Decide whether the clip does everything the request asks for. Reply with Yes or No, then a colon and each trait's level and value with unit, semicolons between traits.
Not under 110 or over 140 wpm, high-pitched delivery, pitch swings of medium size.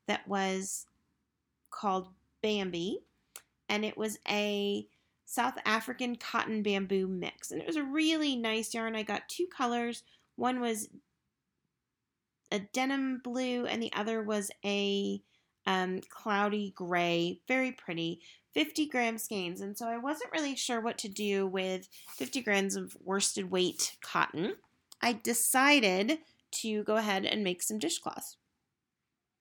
Yes: slow, 135 wpm; high, 215 Hz; average, 3.8 semitones